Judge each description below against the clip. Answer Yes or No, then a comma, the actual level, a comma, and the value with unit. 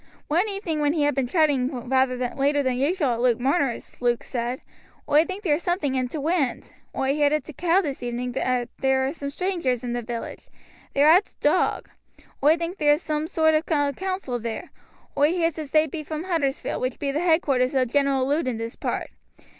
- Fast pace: Yes, fast, 210 wpm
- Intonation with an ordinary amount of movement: Yes, average, 3.9 semitones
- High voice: Yes, very high, 285 Hz